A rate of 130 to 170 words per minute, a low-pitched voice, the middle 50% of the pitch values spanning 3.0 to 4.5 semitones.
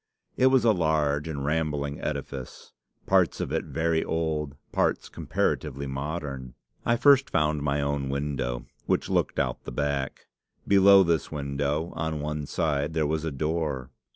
No: average, 155 wpm; very low, 75 Hz; narrow, 2.4 semitones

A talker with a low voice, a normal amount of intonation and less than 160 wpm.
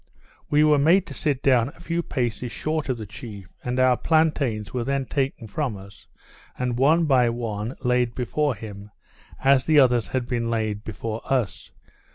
No: low, 125 Hz; average, 3.9 semitones; average, 180 wpm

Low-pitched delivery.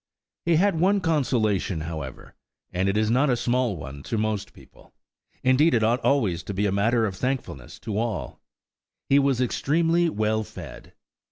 Yes: low, 115 Hz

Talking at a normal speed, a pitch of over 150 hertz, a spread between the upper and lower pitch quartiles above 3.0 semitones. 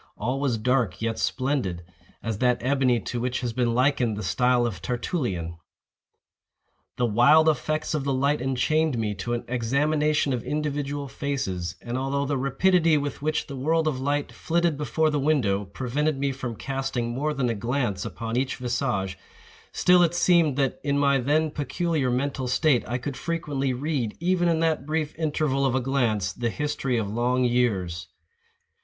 No: average, 170 wpm; low, 135 Hz; average, 3.8 semitones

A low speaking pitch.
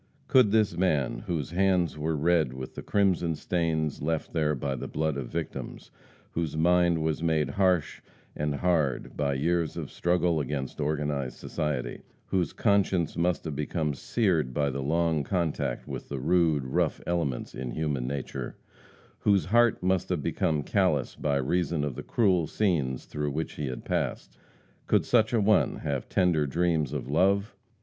Yes: very low, 80 Hz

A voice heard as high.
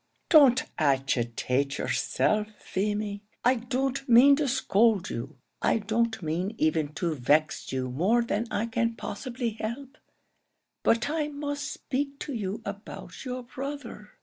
Yes: high, 225 Hz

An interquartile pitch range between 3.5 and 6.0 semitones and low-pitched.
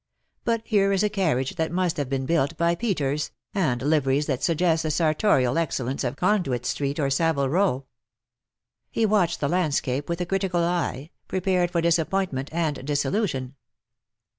No: average, 4.8 semitones; medium, 160 Hz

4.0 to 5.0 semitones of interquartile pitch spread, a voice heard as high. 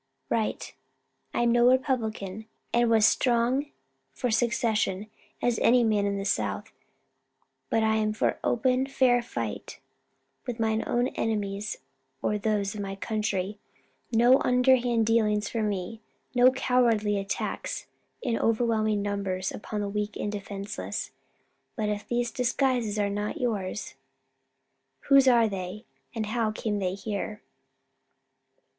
No: narrow, 2.6 semitones; high, 220 Hz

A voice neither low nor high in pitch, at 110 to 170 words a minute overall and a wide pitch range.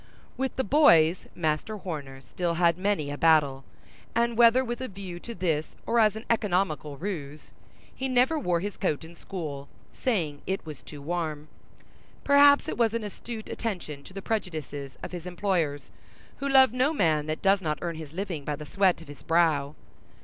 No: medium, 175 Hz; average, 185 wpm; wide, 6.2 semitones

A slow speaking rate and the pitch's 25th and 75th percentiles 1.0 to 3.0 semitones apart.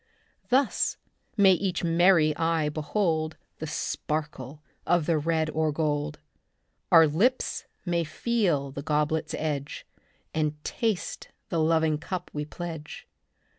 Yes: slow, 120 wpm; narrow, 2.4 semitones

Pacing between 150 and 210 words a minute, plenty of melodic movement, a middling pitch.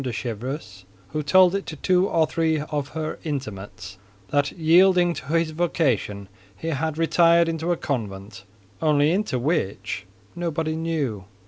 No: average, 140 wpm; wide, 6.4 semitones; medium, 155 Hz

